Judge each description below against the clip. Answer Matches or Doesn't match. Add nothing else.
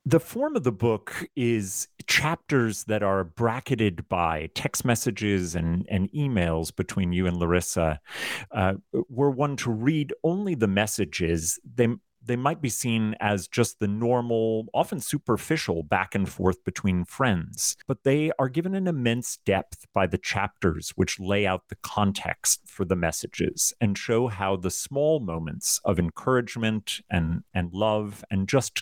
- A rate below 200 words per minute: Matches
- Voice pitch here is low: Matches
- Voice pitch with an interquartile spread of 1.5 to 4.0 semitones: Doesn't match